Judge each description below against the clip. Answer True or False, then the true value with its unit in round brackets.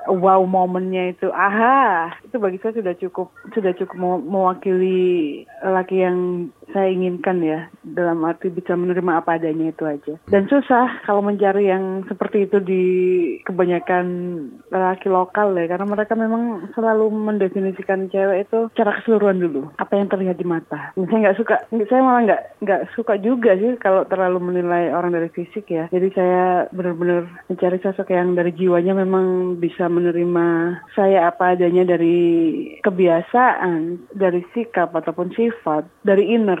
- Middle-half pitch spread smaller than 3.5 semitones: True (2.5 semitones)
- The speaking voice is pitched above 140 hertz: True (185 Hz)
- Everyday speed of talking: False (150 wpm)